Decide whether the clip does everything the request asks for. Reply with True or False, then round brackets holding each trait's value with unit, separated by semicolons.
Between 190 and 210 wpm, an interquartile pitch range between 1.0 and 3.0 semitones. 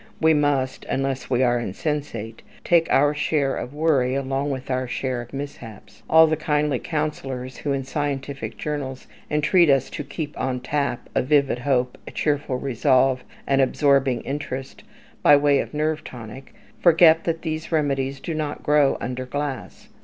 False (160 wpm; 2.5 semitones)